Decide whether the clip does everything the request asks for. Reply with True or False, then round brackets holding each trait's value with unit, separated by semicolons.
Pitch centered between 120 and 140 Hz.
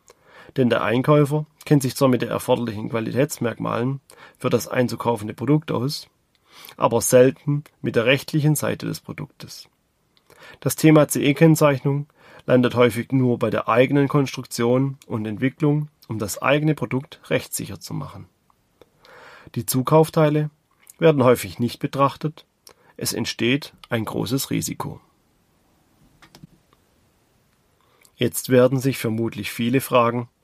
True (135 Hz)